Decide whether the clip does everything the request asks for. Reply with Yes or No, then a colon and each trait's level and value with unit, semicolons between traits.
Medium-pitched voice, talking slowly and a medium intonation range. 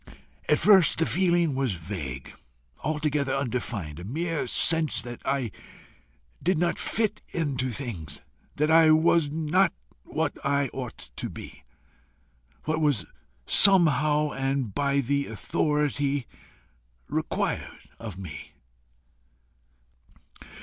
Yes: medium, 145 Hz; slow, 110 wpm; average, 4.4 semitones